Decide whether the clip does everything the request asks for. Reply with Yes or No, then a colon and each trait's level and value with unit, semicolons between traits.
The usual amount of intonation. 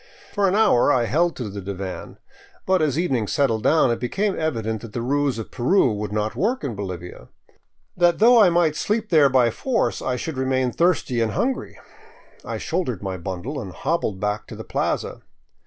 No: wide, 8.1 semitones